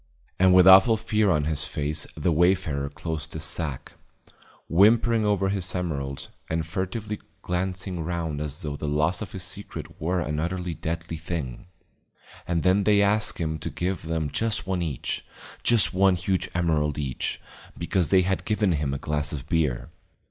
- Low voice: Yes, very low, 85 Hz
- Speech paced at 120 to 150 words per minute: No, average, 170 wpm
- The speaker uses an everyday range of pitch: Yes, average, 3.9 semitones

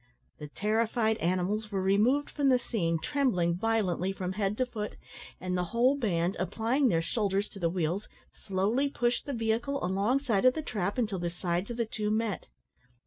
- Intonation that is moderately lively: Yes, average, 4.6 semitones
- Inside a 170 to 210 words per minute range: Yes, average, 180 wpm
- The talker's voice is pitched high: Yes, high, 210 Hz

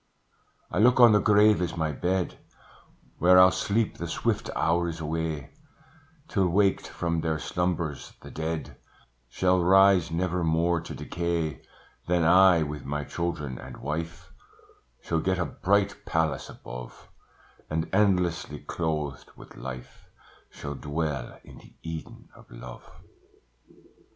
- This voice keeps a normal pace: No, slow, 130 wpm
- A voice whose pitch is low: Yes, very low, 85 Hz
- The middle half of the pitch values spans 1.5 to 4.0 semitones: Yes, average, 2.8 semitones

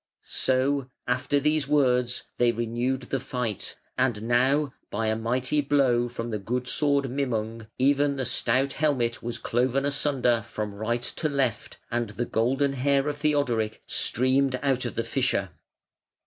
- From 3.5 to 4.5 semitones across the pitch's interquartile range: No, average, 2.8 semitones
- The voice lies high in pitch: No, low, 125 Hz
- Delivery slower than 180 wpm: Yes, average, 150 wpm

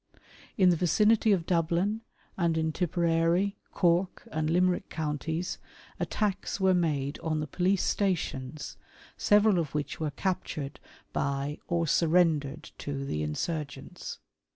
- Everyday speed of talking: No, slow, 130 wpm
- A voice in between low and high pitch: Yes, medium, 165 Hz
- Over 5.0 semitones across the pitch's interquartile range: No, average, 3.4 semitones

